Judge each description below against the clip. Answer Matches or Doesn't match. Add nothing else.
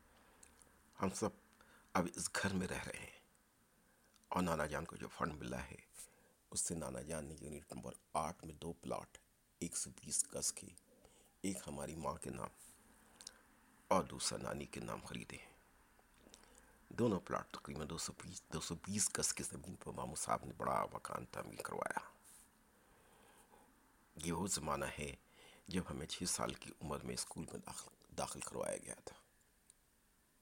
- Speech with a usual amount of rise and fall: Matches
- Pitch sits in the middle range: Doesn't match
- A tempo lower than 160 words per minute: Doesn't match